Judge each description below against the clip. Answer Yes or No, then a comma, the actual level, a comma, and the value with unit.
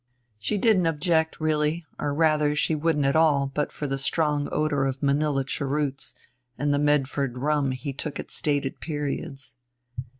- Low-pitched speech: No, medium, 145 Hz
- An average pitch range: No, narrow, 1.9 semitones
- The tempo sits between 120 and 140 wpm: No, average, 160 wpm